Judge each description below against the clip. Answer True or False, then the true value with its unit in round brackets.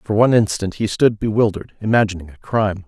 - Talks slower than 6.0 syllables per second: False (6.6 syllables/s)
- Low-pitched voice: True (105 Hz)